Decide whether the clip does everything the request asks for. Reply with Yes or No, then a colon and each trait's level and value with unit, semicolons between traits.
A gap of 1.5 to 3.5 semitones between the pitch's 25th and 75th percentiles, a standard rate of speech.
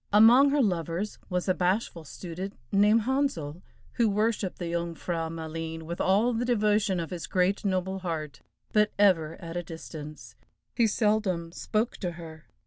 No: average, 4.2 semitones; average, 160 wpm